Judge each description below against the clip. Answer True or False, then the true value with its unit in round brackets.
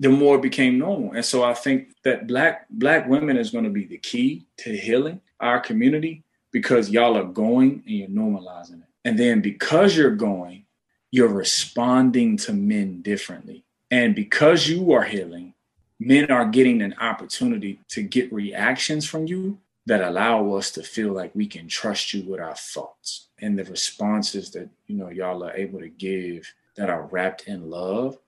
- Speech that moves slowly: False (180 wpm)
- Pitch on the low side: True (125 Hz)